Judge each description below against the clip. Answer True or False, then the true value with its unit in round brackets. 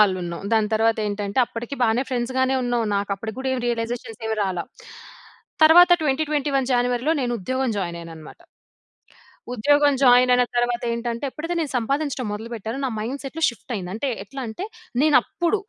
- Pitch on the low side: False (240 Hz)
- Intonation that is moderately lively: True (3.7 semitones)